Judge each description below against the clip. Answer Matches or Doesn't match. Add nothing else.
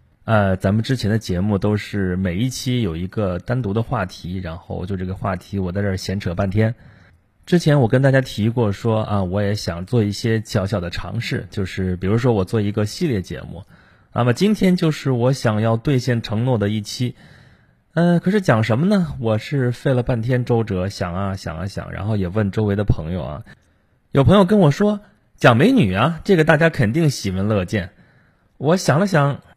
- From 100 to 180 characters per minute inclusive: Doesn't match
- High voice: Doesn't match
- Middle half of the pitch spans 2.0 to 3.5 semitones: Doesn't match